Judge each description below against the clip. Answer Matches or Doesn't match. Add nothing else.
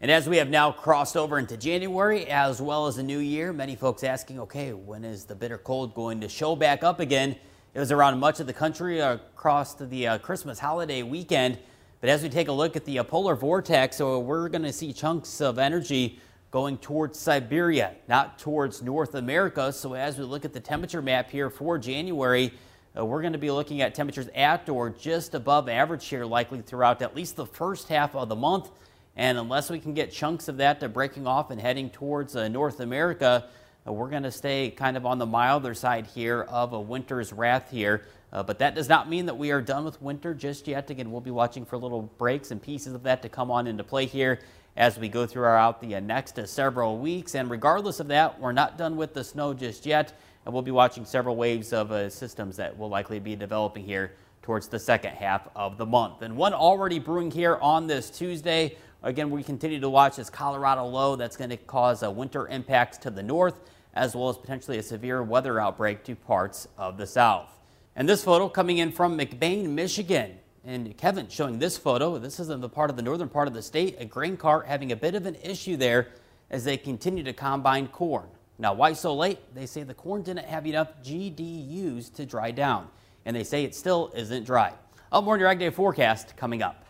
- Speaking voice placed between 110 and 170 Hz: Matches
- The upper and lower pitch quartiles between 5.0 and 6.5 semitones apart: Doesn't match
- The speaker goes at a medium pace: Doesn't match